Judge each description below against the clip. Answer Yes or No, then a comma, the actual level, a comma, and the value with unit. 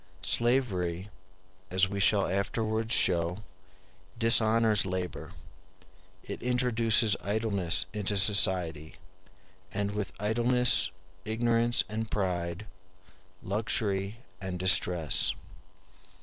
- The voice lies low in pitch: Yes, low, 105 Hz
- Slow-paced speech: Yes, slow, 80 wpm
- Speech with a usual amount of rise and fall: Yes, average, 3.3 semitones